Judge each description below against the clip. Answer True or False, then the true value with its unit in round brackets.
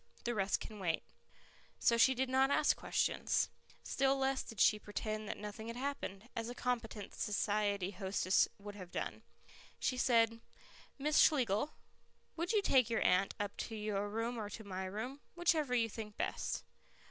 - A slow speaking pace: False (170 wpm)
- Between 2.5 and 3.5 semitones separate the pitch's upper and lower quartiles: False (3.9 semitones)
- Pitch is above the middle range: True (225 Hz)